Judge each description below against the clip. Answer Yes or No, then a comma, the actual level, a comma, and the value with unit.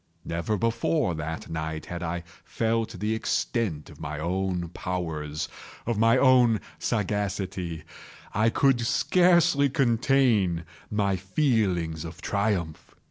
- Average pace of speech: No, slow, 105 wpm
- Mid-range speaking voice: No, low, 100 Hz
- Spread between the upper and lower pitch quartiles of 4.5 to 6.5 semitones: Yes, wide, 5.5 semitones